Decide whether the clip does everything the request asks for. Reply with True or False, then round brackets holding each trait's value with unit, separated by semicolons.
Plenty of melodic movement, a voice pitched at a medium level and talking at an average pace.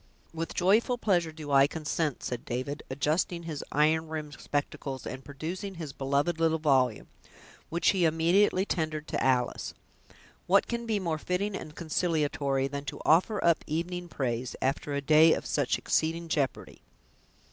False (3.4 semitones; 155 Hz; 155 wpm)